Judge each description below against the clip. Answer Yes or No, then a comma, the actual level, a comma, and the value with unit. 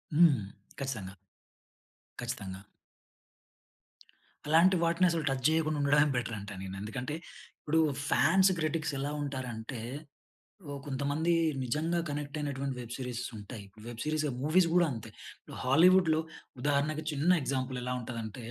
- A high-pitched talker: No, medium, 140 Hz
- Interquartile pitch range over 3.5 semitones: Yes, average, 4.2 semitones